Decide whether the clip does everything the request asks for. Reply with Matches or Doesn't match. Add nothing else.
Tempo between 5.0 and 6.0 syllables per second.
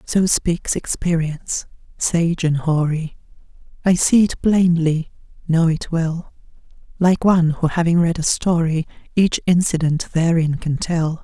Doesn't match